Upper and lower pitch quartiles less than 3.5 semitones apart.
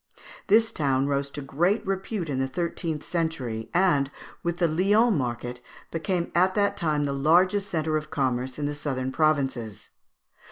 No: average, 4.6 semitones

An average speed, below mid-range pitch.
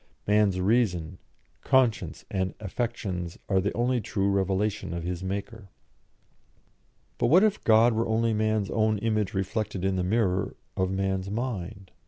Yes: average, 145 wpm; low, 100 Hz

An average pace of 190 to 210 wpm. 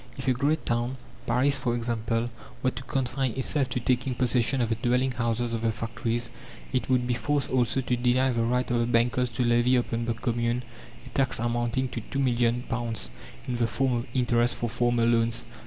Yes: average, 195 wpm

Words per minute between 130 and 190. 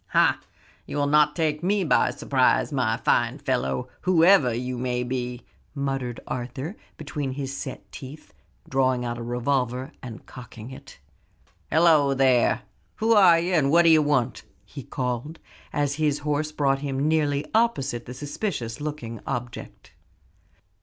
Yes: average, 140 wpm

